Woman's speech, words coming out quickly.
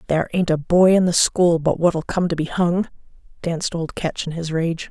Yes: female; fast, 235 wpm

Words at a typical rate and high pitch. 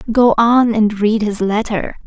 Yes: average, 175 wpm; high, 220 Hz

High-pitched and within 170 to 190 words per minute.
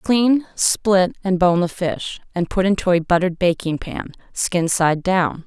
No: medium, 180 Hz; average, 175 wpm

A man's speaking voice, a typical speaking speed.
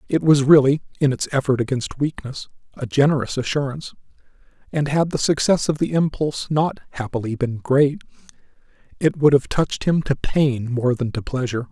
Yes: male; average, 170 wpm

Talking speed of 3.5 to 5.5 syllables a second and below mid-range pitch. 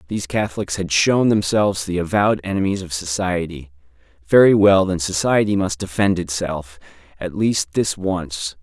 Yes: 5.0 syllables/s; very low, 90 Hz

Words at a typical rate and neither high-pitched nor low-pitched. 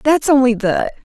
No: average, 155 wpm; very high, 260 Hz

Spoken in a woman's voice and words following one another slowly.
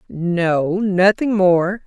Yes: female; slow, 95 wpm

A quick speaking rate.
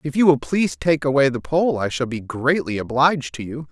Yes: fast, 240 wpm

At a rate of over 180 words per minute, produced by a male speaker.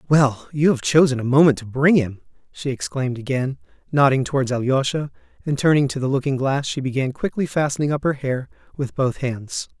Yes: average, 190 wpm; male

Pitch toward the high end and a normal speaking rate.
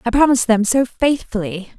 Yes: high, 230 Hz; average, 170 wpm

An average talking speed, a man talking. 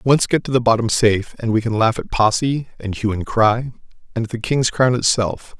No: fast, 235 wpm; male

